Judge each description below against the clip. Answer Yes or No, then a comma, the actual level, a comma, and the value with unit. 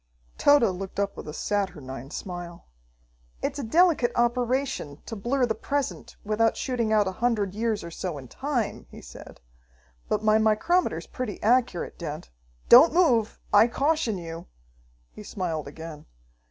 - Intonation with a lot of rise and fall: Yes, wide, 5.9 semitones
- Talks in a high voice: Yes, high, 215 Hz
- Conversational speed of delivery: Yes, average, 150 wpm